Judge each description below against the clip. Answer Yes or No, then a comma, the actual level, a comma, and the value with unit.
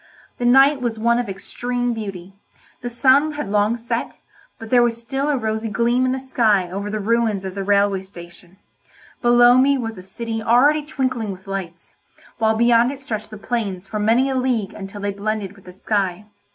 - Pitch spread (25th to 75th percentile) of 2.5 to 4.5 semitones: Yes, average, 3.5 semitones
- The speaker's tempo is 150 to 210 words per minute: Yes, average, 195 wpm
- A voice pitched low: No, high, 225 Hz